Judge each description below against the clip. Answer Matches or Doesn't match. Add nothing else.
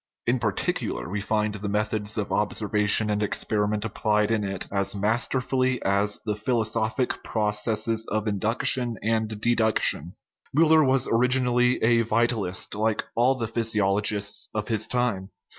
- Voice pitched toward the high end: Doesn't match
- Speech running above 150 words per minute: Doesn't match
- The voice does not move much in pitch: Matches